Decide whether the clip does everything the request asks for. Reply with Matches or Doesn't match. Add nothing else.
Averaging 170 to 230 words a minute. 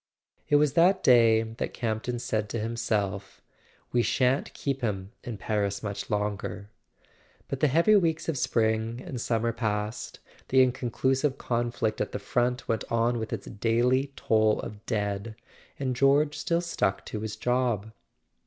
Doesn't match